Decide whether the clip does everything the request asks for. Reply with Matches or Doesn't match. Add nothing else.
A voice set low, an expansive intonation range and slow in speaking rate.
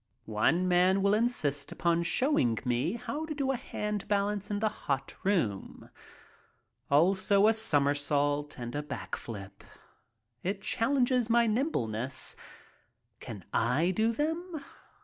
Doesn't match